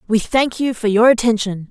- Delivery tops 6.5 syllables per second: No, 5.2 syllables/s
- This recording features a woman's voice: Yes, female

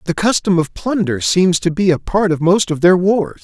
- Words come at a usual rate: No, fast, 245 wpm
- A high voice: No, medium, 175 Hz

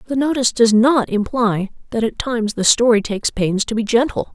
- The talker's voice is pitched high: Yes, high, 230 Hz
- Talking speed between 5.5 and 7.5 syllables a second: Yes, 5.7 syllables/s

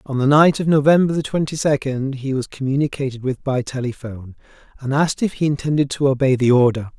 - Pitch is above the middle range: No, low, 135 Hz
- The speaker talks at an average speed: Yes, average, 190 wpm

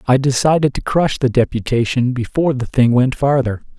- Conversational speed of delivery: Yes, average, 175 wpm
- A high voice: No, low, 130 Hz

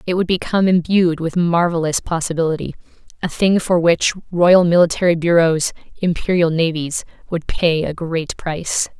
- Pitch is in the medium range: Yes, medium, 170 Hz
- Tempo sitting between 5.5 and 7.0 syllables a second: No, 5.0 syllables/s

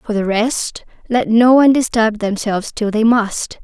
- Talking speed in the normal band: Yes, average, 165 wpm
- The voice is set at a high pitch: Yes, high, 225 Hz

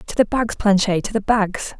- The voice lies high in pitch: Yes, high, 210 Hz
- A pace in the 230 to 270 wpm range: Yes, fast, 235 wpm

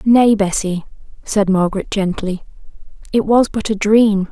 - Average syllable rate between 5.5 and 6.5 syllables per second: No, 4.4 syllables/s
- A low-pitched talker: No, high, 205 Hz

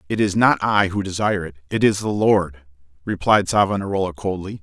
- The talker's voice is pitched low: Yes, very low, 95 Hz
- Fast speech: No, average, 180 wpm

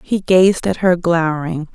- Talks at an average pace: Yes, average, 170 wpm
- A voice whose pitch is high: No, medium, 175 Hz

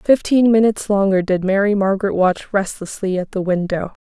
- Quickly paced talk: No, average, 165 wpm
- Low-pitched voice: No, high, 200 Hz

